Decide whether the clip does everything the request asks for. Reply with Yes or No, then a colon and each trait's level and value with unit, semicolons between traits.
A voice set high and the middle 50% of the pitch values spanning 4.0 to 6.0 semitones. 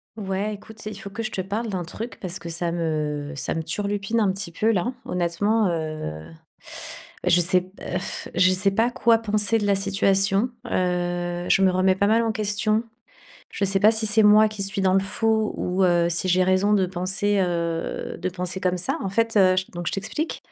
No: high, 195 Hz; average, 2.9 semitones